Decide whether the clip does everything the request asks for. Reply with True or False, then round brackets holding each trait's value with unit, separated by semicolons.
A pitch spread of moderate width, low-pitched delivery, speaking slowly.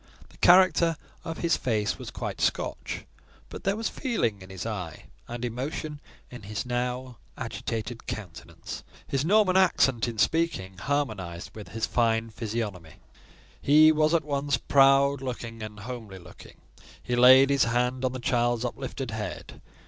False (4.5 semitones; 125 Hz; 150 wpm)